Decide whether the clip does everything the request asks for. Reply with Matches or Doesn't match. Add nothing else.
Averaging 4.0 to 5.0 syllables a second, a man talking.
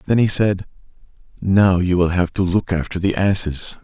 Matches